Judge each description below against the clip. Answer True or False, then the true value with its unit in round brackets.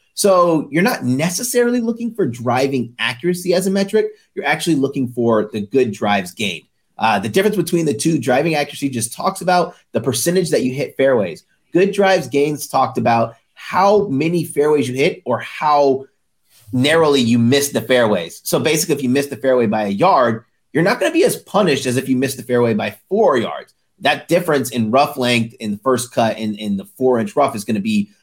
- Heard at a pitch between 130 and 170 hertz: True (140 Hz)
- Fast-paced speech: True (210 wpm)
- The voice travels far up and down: True (6.1 semitones)